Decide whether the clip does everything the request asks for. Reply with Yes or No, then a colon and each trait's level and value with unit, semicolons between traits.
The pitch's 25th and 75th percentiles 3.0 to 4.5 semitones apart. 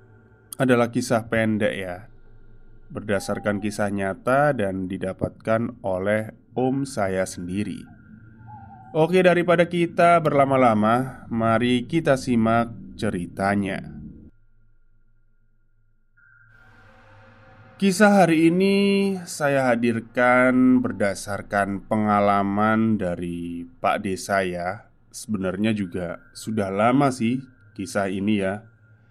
Yes: average, 3.5 semitones